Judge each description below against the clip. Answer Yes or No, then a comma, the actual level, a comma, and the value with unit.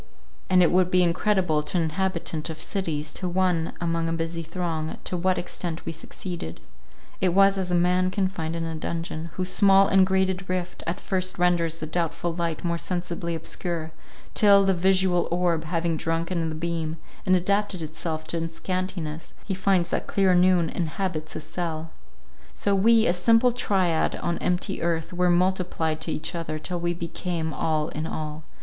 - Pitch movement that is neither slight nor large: No, narrow, 2.2 semitones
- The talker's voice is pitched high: No, medium, 175 Hz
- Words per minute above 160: Yes, average, 180 wpm